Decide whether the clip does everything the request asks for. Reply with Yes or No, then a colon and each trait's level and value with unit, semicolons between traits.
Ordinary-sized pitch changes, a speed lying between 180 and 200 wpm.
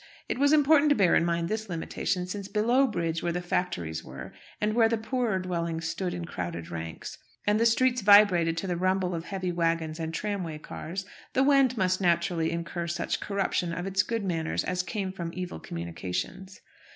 Yes: average, 3.9 semitones; average, 190 wpm